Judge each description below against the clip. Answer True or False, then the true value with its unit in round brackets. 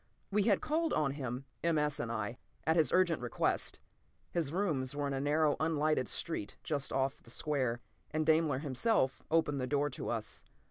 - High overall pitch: False (145 Hz)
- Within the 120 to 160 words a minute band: False (185 wpm)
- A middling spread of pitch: True (3.4 semitones)